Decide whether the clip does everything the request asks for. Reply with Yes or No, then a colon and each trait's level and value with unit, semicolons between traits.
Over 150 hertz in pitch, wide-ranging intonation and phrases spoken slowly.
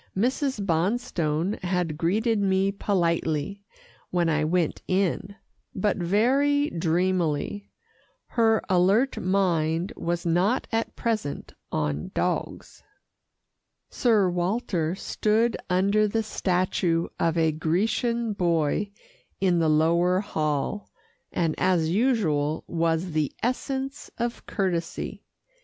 No: medium, 185 Hz; average, 4.4 semitones; slow, 105 wpm